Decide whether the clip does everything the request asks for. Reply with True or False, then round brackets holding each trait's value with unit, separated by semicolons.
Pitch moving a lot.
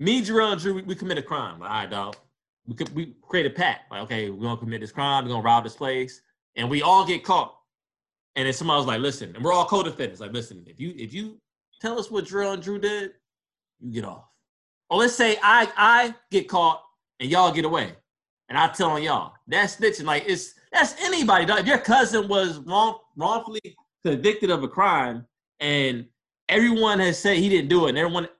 True (7.1 semitones)